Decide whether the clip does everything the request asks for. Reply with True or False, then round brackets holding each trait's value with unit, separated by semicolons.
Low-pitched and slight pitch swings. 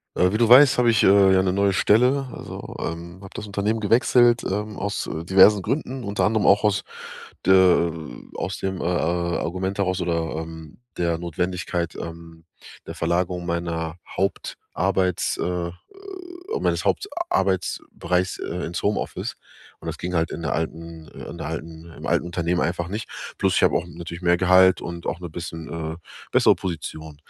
False (90 Hz; 3.0 semitones)